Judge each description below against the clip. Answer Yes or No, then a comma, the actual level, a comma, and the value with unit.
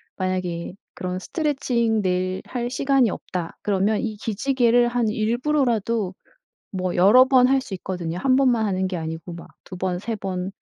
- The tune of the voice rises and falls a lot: No, average, 4.9 semitones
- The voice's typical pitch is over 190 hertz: Yes, high, 210 Hz